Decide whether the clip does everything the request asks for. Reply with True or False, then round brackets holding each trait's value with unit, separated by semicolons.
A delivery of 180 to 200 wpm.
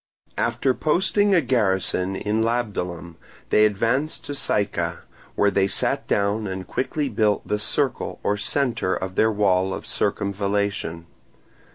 False (135 wpm)